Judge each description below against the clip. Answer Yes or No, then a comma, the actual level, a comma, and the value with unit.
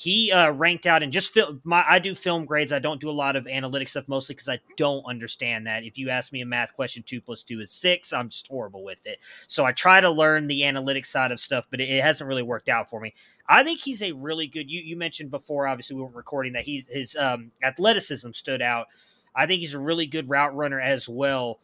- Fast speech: Yes, fast, 255 wpm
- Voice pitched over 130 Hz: Yes, medium, 140 Hz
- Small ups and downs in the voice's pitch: No, average, 4.0 semitones